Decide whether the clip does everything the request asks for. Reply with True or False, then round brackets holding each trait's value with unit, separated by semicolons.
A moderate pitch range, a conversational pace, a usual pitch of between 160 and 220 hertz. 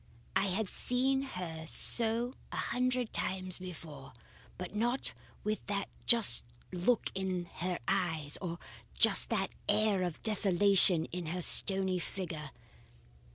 False (3.9 semitones; 125 wpm; 190 Hz)